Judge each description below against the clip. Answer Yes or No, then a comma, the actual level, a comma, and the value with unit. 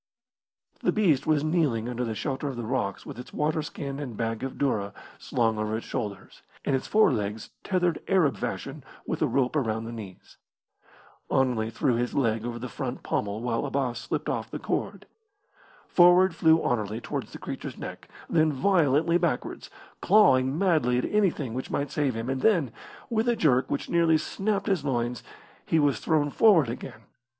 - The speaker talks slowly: No, average, 175 wpm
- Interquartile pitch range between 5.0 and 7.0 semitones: Yes, wide, 5.4 semitones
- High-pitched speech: No, low, 135 Hz